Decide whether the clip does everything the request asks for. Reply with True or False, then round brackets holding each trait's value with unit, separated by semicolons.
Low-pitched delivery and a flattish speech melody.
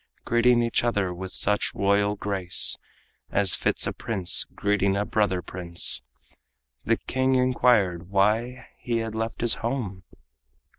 False (105 Hz; 3.7 semitones)